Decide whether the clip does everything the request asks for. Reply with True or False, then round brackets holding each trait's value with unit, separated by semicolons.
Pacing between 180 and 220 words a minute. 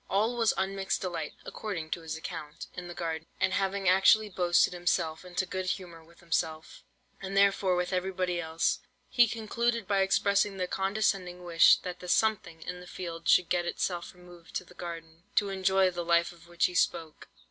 True (185 wpm)